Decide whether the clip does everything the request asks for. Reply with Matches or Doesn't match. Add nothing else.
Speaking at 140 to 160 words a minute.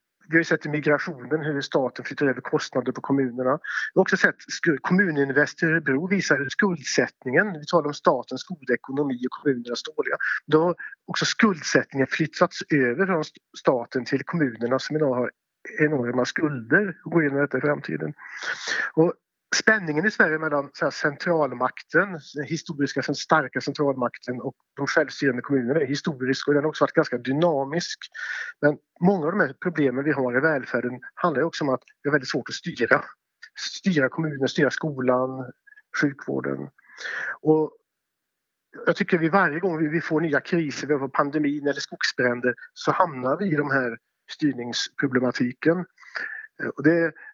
Matches